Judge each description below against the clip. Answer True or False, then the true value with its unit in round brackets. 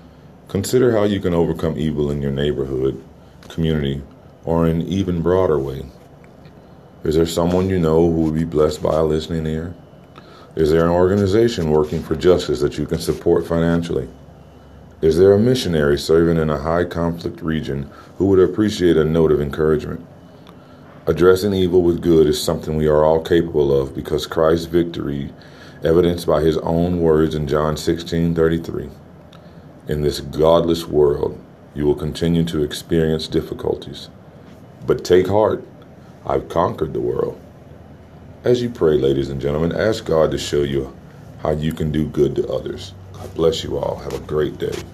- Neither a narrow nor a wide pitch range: False (2.1 semitones)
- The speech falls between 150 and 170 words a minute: True (165 wpm)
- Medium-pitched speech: False (80 Hz)